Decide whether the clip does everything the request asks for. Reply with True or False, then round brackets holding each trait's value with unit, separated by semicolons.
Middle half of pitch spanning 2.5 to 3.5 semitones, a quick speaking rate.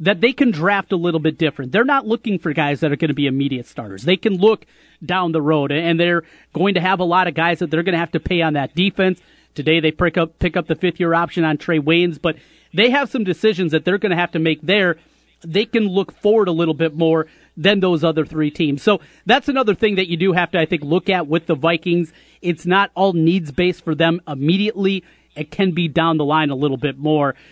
True (3.2 semitones; 255 wpm)